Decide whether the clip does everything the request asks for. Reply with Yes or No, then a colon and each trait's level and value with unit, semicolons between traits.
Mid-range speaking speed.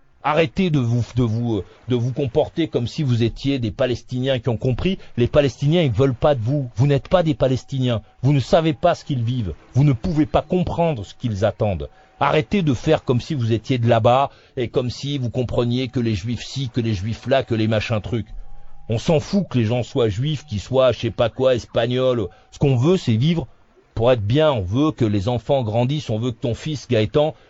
No: fast, 230 wpm